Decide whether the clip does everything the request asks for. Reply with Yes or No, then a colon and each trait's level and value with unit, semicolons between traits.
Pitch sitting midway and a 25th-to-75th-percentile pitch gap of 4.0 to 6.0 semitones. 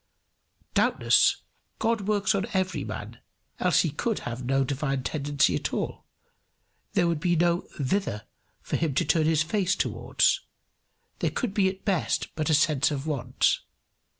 Yes: medium, 155 Hz; wide, 5.6 semitones